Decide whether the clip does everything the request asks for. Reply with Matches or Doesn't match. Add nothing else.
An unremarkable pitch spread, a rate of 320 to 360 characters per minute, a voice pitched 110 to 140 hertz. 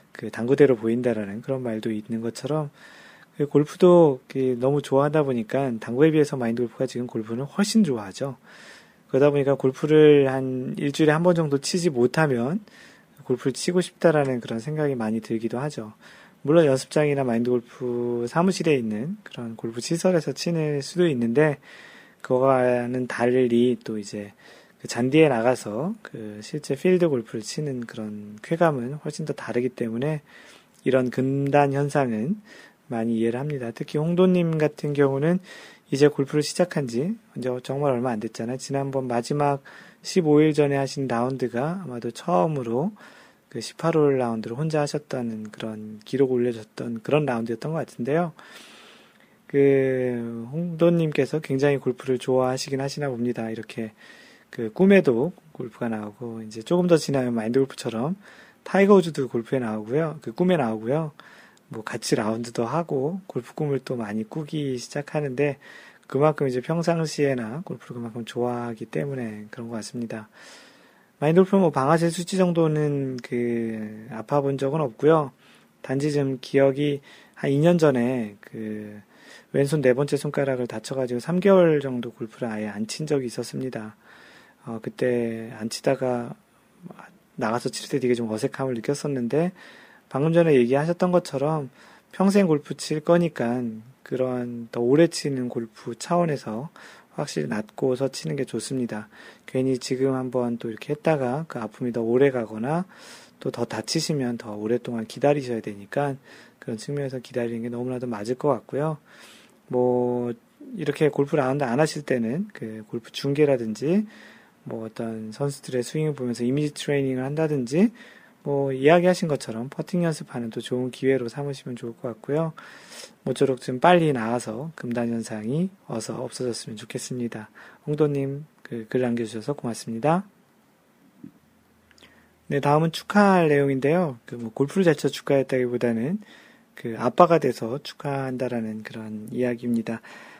Matches